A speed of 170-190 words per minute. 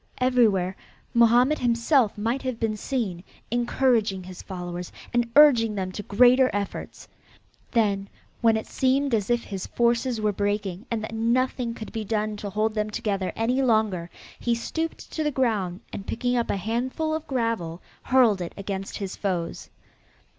No: average, 160 wpm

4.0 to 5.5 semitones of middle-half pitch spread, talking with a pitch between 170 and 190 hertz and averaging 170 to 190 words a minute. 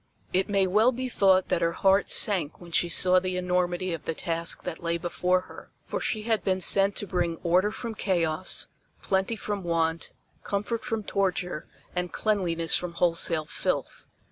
No: average, 2.8 semitones; medium, 185 Hz; average, 175 wpm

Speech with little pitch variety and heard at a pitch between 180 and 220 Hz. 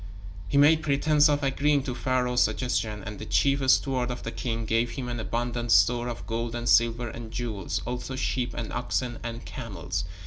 No: narrow, 2.2 semitones; low, 120 Hz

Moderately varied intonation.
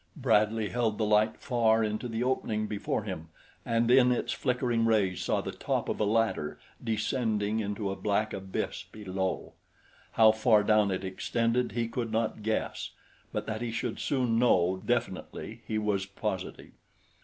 No: narrow, 2.1 semitones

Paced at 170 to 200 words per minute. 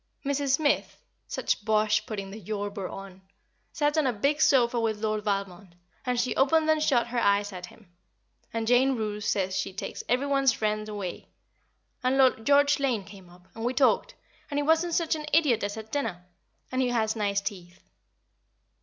Yes: average, 185 wpm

